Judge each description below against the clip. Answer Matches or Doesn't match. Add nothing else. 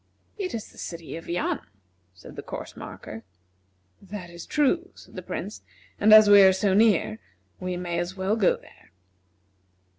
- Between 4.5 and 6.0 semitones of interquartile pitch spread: Doesn't match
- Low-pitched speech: Doesn't match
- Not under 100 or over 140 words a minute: Doesn't match